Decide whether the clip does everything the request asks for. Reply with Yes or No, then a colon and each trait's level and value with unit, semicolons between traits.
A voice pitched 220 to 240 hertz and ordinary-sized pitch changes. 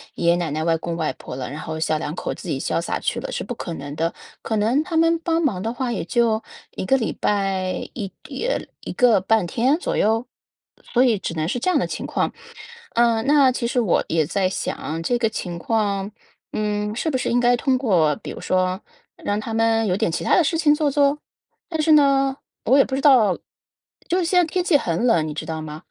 No: high, 225 Hz; wide, 7.3 semitones